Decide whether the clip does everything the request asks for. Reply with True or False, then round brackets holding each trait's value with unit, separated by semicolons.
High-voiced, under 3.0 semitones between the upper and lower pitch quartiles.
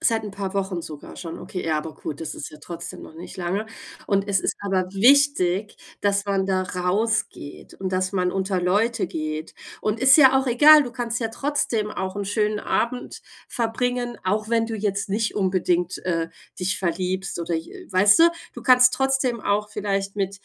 False (200 Hz; 3.7 semitones)